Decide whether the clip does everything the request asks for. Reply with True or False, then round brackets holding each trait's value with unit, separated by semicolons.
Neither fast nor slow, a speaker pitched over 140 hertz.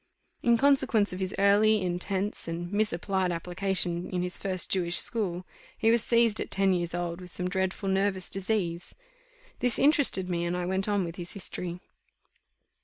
True (170 wpm; 190 Hz)